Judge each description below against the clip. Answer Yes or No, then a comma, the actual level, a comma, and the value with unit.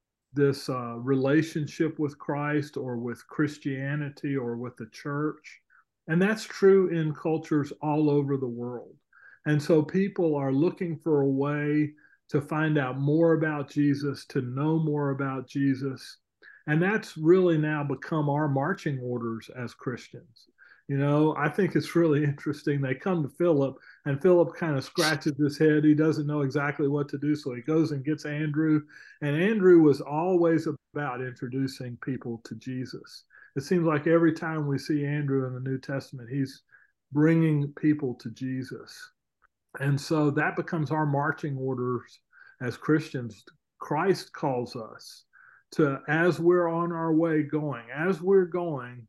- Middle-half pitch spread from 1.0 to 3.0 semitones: Yes, average, 2.7 semitones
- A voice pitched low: No, medium, 150 Hz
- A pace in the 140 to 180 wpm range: Yes, average, 160 wpm